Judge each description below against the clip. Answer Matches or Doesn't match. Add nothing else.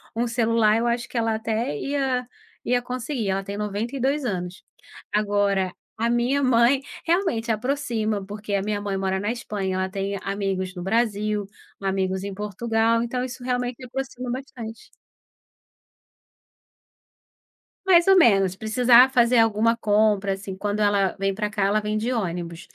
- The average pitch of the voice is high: Matches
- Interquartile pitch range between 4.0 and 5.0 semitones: Doesn't match